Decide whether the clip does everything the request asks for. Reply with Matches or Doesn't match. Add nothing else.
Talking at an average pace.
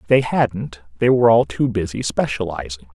Matches